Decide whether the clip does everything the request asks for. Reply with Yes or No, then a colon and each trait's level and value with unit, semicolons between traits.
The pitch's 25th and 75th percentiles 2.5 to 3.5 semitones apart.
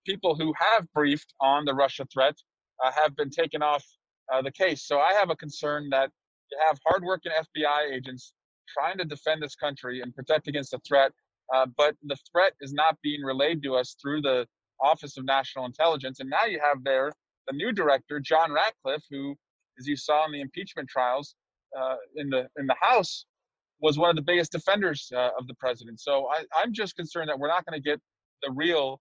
Yes: average, 2.9 semitones